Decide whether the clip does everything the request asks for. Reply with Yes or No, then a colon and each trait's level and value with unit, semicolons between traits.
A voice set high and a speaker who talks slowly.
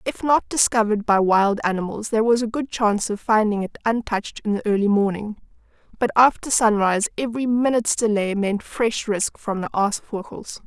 No: high, 215 Hz; average, 175 wpm